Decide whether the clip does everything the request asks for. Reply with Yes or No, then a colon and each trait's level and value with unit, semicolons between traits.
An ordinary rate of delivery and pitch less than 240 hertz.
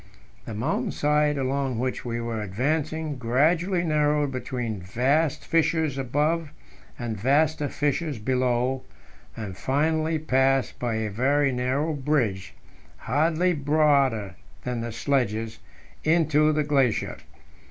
No: slow, 115 wpm; low, 135 Hz